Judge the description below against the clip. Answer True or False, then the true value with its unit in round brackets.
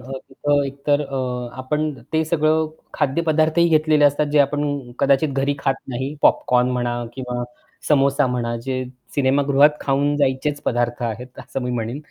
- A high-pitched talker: False (135 Hz)